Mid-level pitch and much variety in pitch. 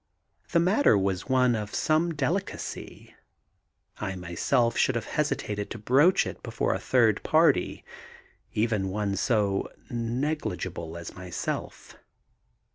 No: low, 115 Hz; wide, 6.7 semitones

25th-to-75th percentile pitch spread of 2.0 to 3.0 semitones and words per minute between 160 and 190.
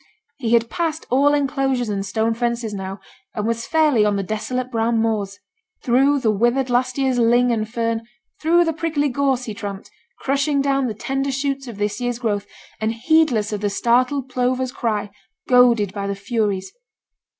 No: average, 3.9 semitones; average, 175 wpm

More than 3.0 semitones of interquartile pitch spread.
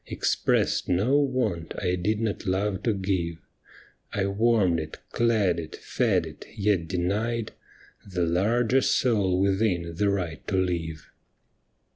Yes: average, 3.9 semitones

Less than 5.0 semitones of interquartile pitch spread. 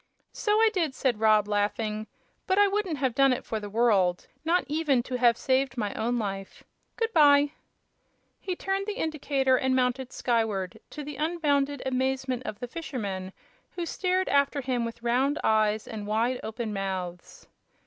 No: average, 5.3 semitones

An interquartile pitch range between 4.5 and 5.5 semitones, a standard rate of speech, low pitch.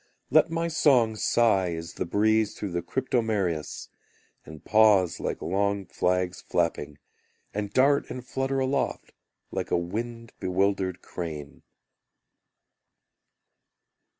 No: average, 5.1 semitones; slow, 110 wpm; low, 100 Hz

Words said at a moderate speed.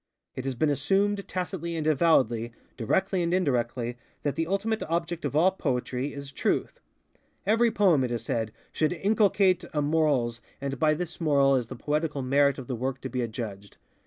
Yes: average, 180 wpm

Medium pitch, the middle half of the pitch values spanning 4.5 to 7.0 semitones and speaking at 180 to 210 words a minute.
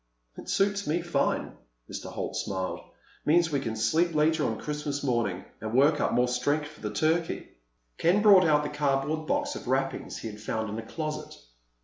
Yes: medium, 150 Hz; wide, 5.5 semitones; average, 185 wpm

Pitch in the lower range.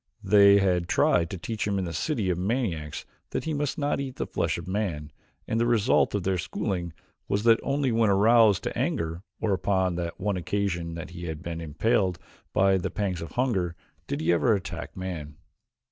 Yes: very low, 95 Hz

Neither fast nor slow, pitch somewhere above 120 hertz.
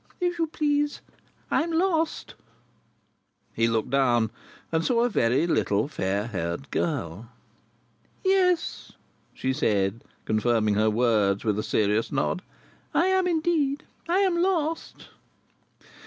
No: slow, 125 wpm; medium, 140 Hz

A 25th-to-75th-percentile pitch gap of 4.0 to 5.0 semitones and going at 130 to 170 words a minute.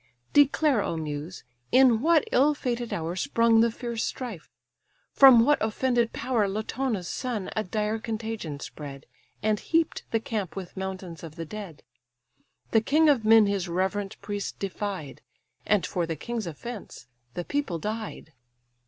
Yes: average, 4.6 semitones; average, 150 wpm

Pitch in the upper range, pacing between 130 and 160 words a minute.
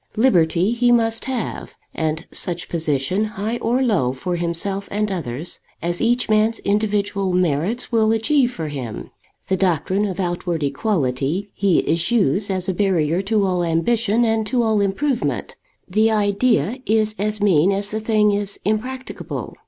Yes: high, 200 Hz; average, 150 wpm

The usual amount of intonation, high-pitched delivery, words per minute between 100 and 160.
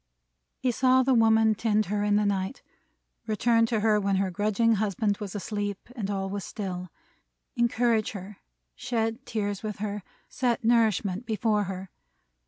No: narrow, 2.3 semitones; high, 210 Hz; average, 155 wpm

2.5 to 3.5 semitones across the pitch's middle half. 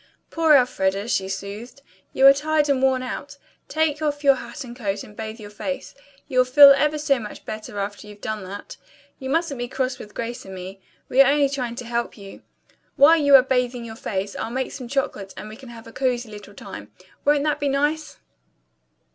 No: average, 4.7 semitones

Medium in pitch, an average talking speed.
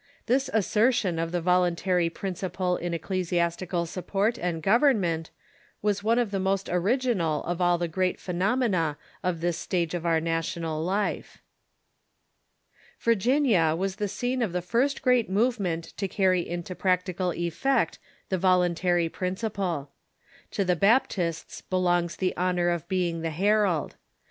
Yes: medium, 180 Hz; average, 145 wpm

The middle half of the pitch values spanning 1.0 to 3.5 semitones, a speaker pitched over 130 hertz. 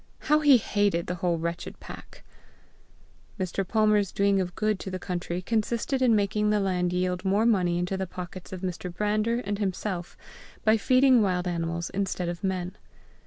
Yes: average, 2.9 semitones; high, 190 Hz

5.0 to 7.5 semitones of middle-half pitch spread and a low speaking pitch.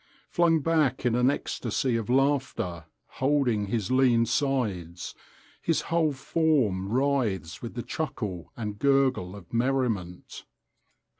Yes: average, 5.3 semitones; low, 125 Hz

